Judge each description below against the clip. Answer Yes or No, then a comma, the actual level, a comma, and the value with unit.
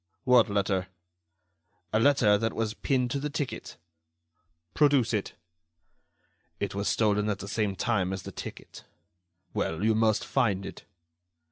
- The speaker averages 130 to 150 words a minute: Yes, average, 140 wpm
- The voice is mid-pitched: No, low, 110 Hz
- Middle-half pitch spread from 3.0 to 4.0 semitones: Yes, average, 3.3 semitones